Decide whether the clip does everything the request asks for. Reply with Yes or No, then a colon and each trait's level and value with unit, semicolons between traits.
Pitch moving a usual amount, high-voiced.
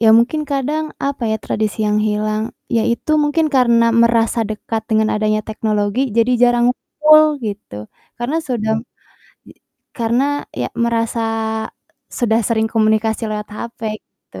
No: narrow, 2.2 semitones; high, 230 Hz